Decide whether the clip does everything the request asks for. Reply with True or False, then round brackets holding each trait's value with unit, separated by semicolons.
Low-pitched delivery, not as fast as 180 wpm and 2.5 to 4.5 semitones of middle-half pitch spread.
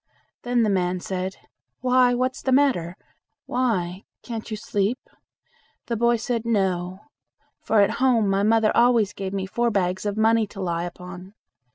False (210 Hz; 160 wpm; 4.0 semitones)